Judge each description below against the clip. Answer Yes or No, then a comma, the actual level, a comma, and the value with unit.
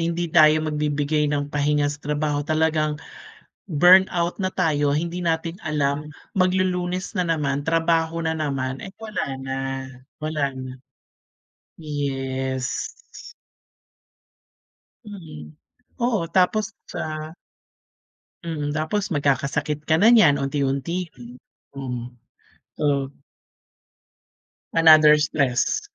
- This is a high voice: No, medium, 155 Hz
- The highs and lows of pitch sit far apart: No, average, 2.9 semitones